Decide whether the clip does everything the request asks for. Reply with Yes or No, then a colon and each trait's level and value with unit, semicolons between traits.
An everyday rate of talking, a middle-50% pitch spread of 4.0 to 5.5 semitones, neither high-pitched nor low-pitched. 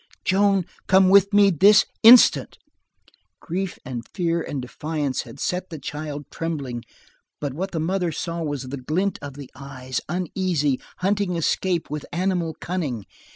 Yes: average, 150 wpm; average, 4.7 semitones; medium, 165 Hz